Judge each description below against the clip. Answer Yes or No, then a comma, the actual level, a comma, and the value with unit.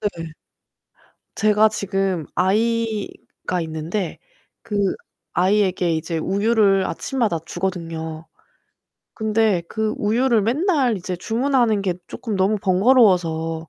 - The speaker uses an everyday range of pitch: Yes, average, 4.1 semitones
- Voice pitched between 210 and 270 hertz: No, high, 200 Hz